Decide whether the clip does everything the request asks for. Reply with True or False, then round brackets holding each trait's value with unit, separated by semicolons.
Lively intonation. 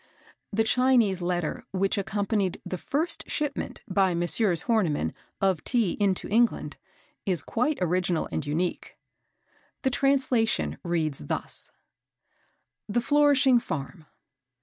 True (5.7 semitones)